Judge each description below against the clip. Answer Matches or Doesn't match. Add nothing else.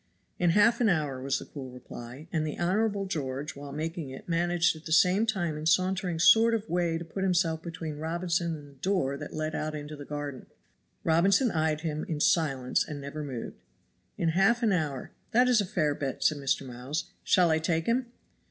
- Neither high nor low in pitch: Matches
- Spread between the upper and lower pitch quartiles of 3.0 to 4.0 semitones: Matches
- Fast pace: Matches